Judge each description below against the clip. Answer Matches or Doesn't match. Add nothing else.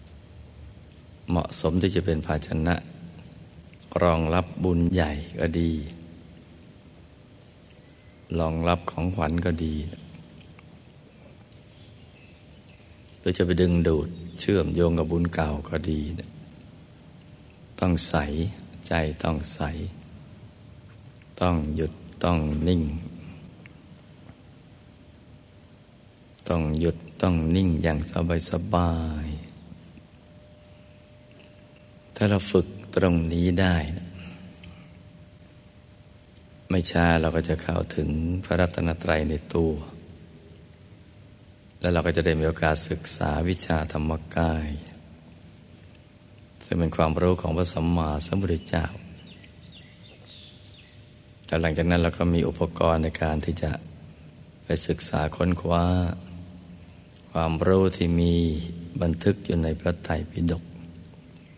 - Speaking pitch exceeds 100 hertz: Doesn't match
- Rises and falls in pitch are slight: Matches